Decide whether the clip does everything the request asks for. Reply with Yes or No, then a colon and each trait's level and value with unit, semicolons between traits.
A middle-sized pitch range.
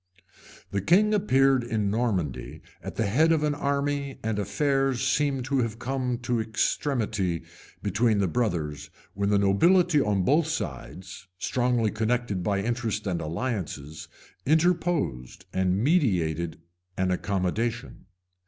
No: wide, 6.3 semitones